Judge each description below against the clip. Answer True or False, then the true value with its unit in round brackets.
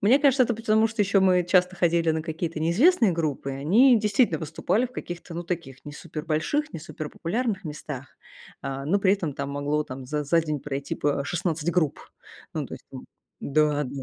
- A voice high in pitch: False (165 Hz)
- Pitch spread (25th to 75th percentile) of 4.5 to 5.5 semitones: True (5.2 semitones)